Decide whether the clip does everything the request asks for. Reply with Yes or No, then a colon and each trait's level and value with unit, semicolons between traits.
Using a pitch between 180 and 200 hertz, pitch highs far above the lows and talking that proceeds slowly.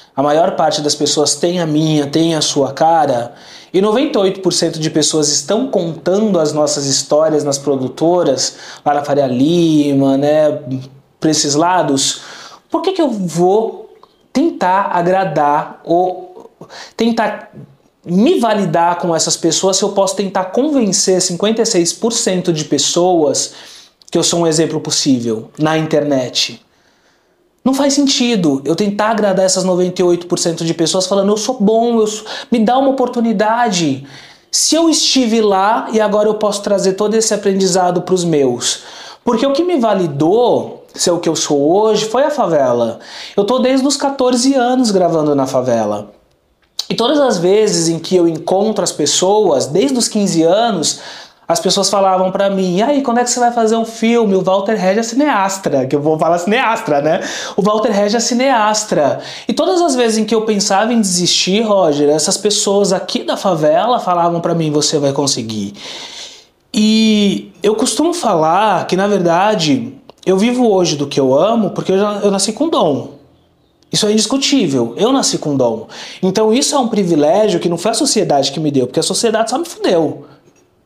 No: high, 190 Hz; wide, 5.9 semitones; average, 170 wpm